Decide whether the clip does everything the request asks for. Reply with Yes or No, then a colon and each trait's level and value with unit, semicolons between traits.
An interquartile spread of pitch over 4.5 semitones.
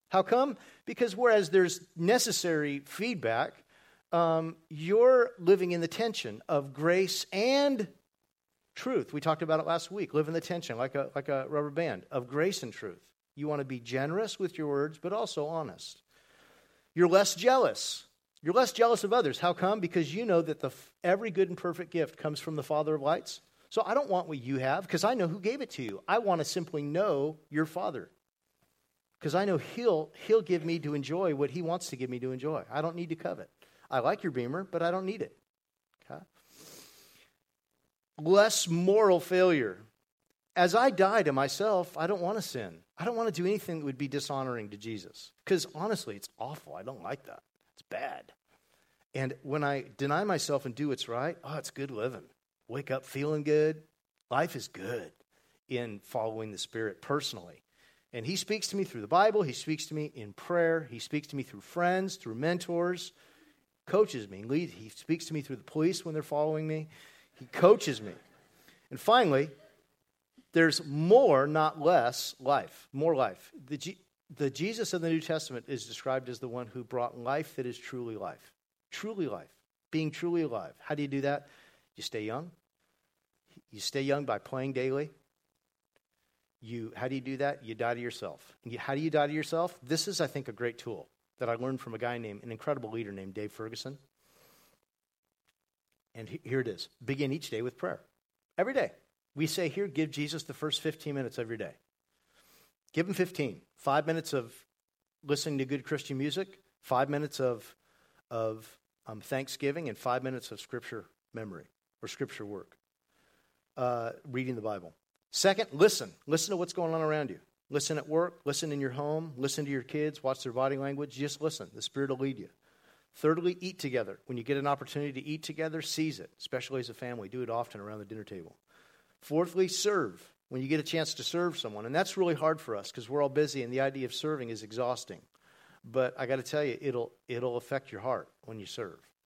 Yes: average, 4.9 semitones